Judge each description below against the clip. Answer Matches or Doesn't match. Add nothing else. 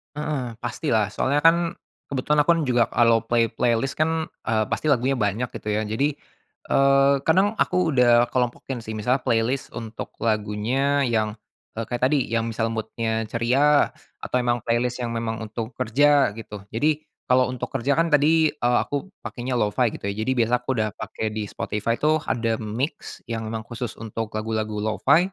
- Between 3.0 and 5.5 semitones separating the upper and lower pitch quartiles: Matches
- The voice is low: Matches